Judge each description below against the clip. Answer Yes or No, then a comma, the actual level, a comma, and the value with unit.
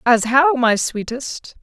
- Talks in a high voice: Yes, very high, 255 Hz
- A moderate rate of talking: Yes, average, 150 wpm